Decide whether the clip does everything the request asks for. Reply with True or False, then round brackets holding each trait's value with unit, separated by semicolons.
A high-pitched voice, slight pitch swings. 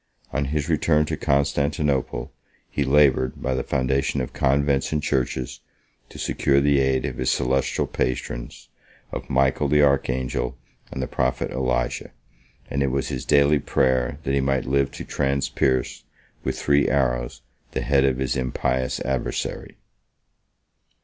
False (65 Hz; 1.7 semitones)